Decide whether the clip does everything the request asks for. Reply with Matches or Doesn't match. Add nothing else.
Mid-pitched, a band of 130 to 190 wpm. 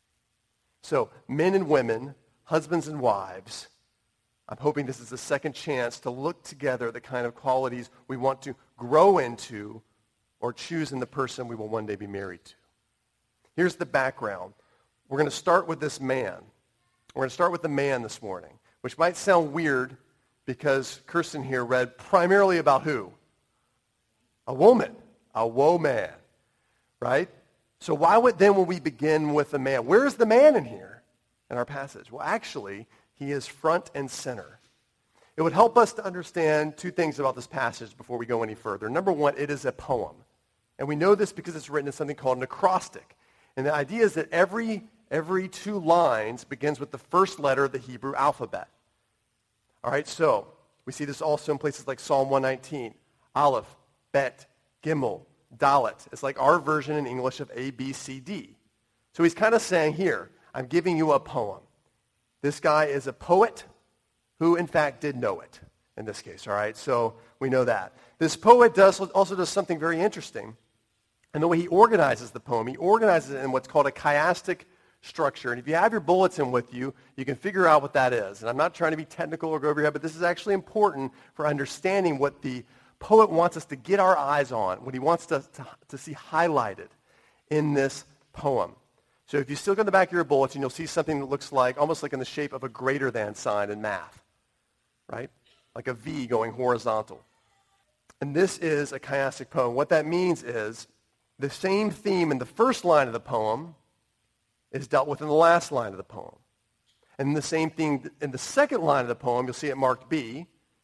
Doesn't match